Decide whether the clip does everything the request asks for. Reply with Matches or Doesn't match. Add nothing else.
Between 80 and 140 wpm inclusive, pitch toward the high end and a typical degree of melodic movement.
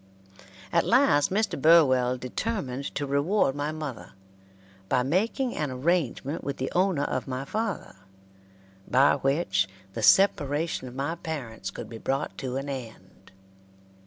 Doesn't match